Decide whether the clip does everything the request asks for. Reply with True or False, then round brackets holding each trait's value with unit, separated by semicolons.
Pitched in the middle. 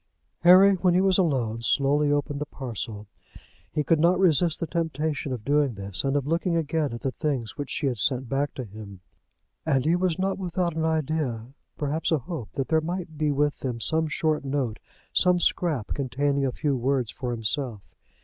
True (145 Hz)